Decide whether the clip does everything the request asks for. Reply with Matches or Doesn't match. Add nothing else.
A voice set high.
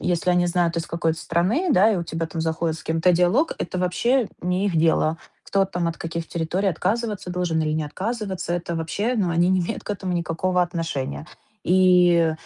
Doesn't match